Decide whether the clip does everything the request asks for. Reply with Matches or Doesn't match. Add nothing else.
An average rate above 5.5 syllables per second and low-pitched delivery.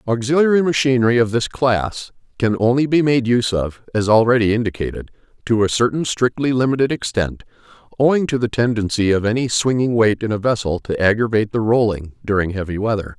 Matches